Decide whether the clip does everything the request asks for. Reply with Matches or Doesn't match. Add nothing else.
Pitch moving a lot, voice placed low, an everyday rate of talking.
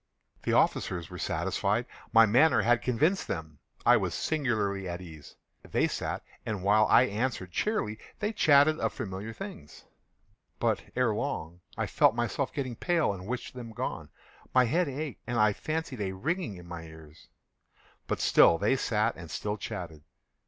Matches